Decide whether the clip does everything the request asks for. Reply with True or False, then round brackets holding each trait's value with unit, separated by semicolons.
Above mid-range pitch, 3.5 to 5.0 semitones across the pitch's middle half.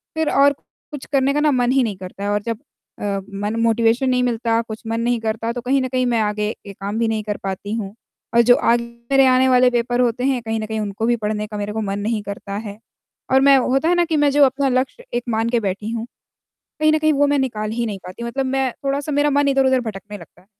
True (235 Hz; 3.8 semitones)